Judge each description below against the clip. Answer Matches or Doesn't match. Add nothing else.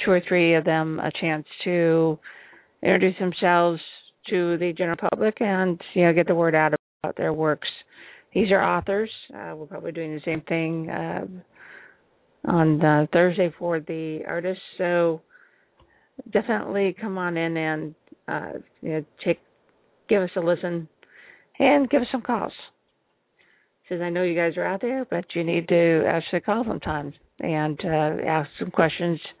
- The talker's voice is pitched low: Doesn't match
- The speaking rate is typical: Matches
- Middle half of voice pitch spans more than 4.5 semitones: Doesn't match